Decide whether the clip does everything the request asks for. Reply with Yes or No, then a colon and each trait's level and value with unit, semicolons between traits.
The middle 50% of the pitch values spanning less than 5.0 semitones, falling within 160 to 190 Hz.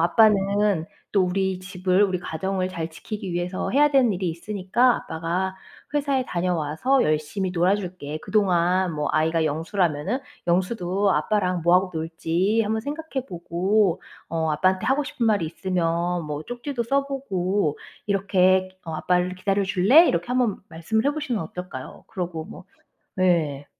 Yes: average, 3.7 semitones; medium, 185 Hz